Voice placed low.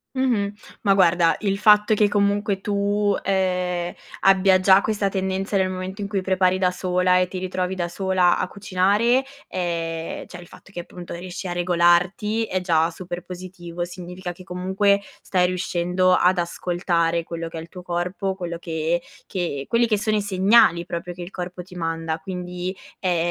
No: medium, 185 Hz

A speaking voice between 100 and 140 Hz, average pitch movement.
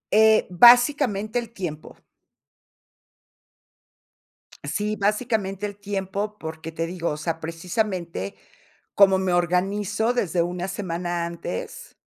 No: high, 190 Hz; average, 3.6 semitones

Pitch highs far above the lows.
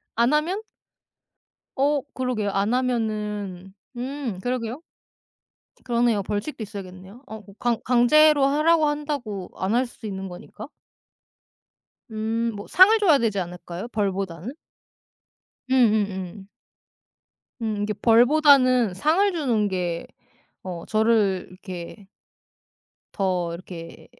No: average, 4.9 semitones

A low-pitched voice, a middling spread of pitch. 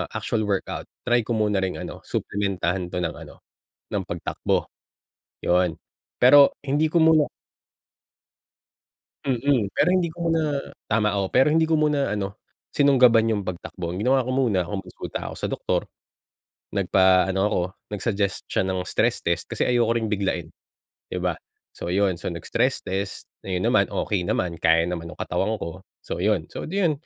No: low, 100 Hz; wide, 6.0 semitones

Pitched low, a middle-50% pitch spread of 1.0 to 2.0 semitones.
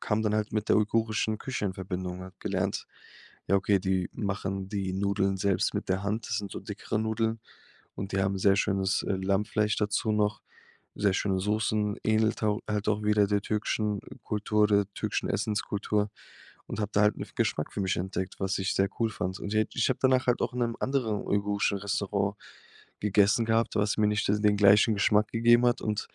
Yes: low, 105 Hz; narrow, 1.7 semitones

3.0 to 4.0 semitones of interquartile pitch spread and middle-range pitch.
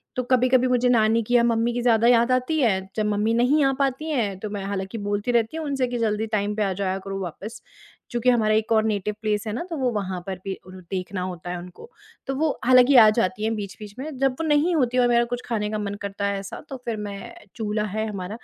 No: average, 3.7 semitones; high, 220 Hz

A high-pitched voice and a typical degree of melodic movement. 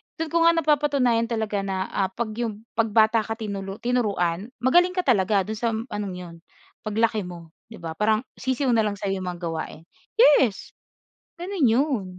Yes: high, 220 Hz; average, 4.5 semitones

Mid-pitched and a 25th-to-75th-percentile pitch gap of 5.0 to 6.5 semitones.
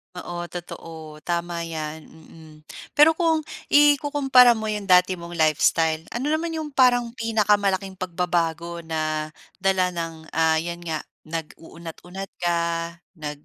Yes: medium, 175 Hz; average, 5.3 semitones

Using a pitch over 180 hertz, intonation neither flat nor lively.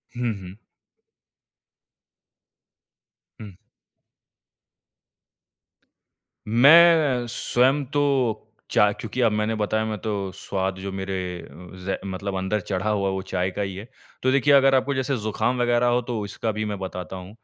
No: low, 105 Hz; average, 4.2 semitones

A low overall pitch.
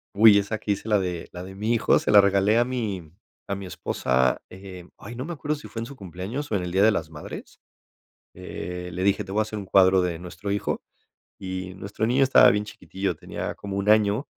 Yes: low, 100 Hz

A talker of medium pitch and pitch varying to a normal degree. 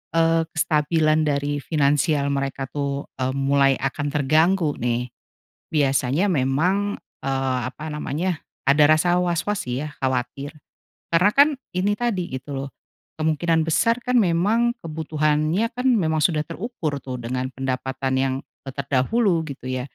Yes: medium, 150 Hz; average, 4.0 semitones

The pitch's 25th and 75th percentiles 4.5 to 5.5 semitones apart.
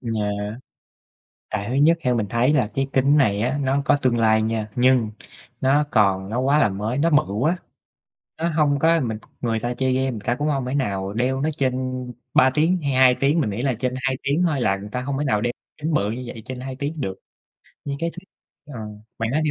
No: average, 4.1 semitones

